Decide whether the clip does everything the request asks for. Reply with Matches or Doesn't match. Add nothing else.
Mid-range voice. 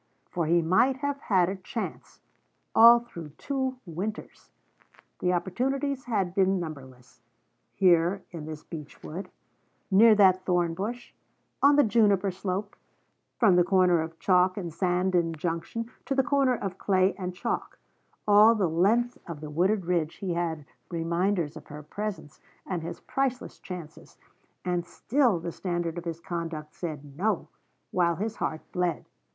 Matches